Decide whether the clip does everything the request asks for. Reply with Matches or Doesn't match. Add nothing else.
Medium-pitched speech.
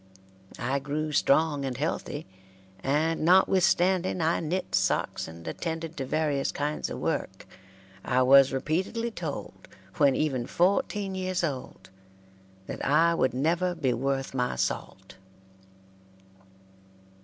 Matches